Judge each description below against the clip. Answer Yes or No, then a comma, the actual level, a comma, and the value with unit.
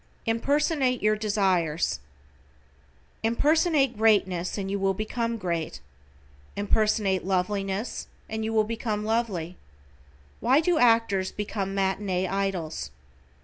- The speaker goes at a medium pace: No, slow, 105 wpm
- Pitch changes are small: No, average, 3.1 semitones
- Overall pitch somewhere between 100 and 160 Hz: No, high, 210 Hz